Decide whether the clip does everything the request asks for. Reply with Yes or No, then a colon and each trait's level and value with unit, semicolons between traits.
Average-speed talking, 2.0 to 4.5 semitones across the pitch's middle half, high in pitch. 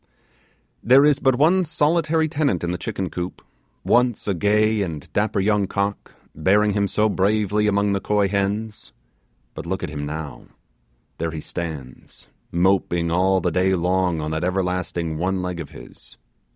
No: average, 165 wpm; average, 3.4 semitones; very low, 95 Hz